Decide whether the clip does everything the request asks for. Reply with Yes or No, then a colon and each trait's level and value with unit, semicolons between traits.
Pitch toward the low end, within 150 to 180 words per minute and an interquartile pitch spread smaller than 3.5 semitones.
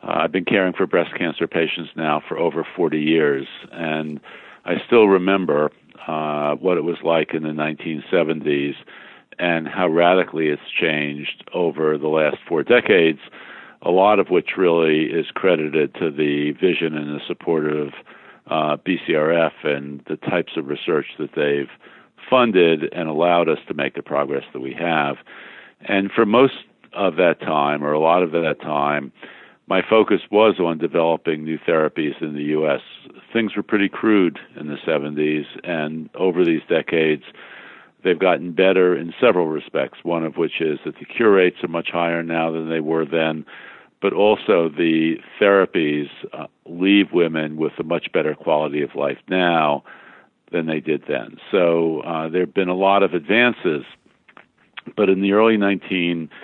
Yes: very low, 80 Hz; average, 165 wpm; average, 3.0 semitones